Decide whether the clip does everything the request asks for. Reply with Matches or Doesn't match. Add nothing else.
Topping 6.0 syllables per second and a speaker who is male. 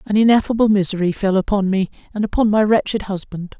Doesn't match